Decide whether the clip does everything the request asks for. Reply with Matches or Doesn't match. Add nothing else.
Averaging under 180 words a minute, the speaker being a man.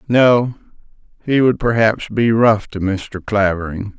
Matches